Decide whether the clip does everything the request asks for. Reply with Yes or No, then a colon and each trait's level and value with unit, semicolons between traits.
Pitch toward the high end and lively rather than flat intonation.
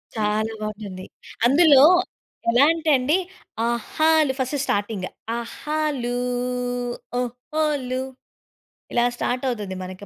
Yes: very high, 250 Hz; wide, 5.7 semitones